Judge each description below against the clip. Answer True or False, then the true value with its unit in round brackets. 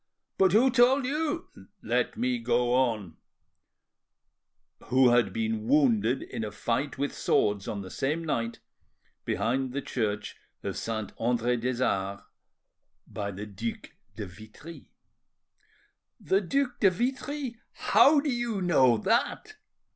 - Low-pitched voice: True (130 Hz)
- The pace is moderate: False (125 wpm)